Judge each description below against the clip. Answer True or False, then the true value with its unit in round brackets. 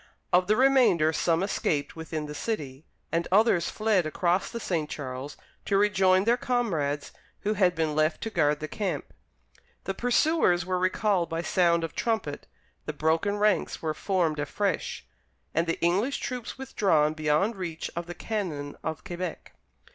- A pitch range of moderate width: True (4.9 semitones)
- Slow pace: False (160 wpm)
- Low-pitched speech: False (175 Hz)